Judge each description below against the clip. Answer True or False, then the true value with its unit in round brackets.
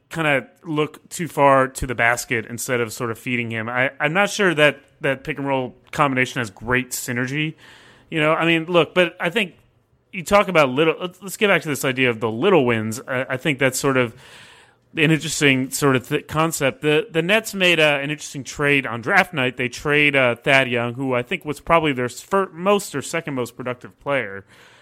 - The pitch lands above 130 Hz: True (140 Hz)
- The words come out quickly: True (220 wpm)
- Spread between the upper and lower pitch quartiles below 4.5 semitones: True (4.0 semitones)